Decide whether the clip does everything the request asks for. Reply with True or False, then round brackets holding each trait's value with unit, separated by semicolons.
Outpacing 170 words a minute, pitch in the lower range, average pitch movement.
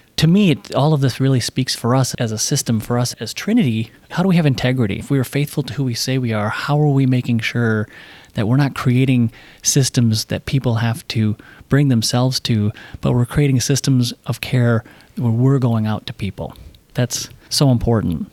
True (205 wpm; 125 Hz; 3.2 semitones)